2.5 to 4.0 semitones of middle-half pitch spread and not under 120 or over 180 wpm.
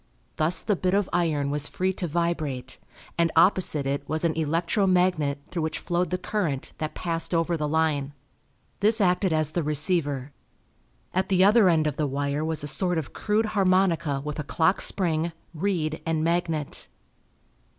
Yes: average, 3.3 semitones; average, 170 wpm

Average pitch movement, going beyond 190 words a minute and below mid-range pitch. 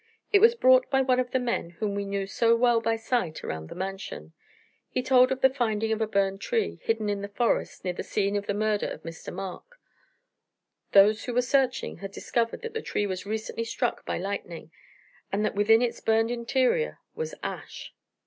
No: average, 4.0 semitones; fast, 205 wpm; high, 225 Hz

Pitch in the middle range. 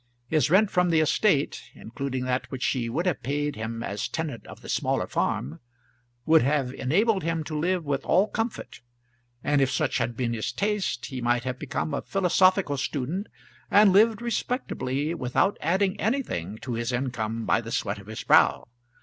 Yes: medium, 145 Hz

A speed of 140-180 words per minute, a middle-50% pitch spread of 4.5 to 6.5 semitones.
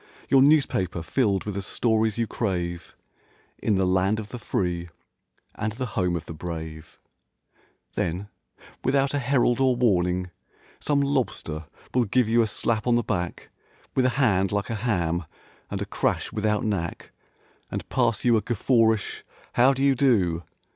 Yes: average, 160 wpm; average, 5.3 semitones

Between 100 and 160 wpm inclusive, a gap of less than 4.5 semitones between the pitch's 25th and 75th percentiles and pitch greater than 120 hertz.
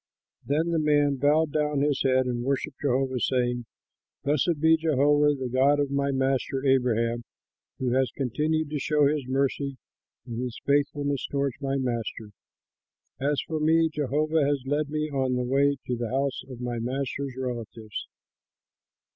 Yes: average, 155 wpm; narrow, 2.4 semitones; medium, 140 Hz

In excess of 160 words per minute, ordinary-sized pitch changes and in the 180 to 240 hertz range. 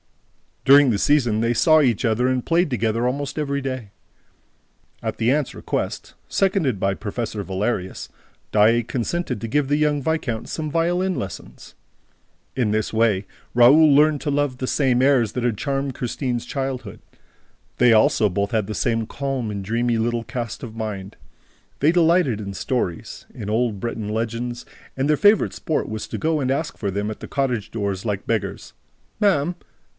No: average, 170 wpm; average, 4.7 semitones; low, 120 Hz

